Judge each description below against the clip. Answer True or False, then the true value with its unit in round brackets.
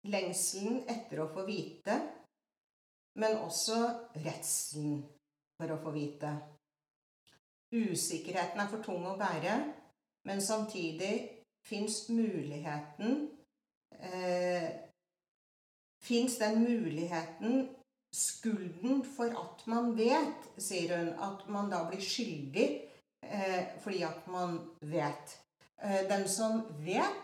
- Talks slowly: True (95 wpm)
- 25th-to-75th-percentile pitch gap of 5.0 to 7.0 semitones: True (5.3 semitones)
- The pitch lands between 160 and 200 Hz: True (190 Hz)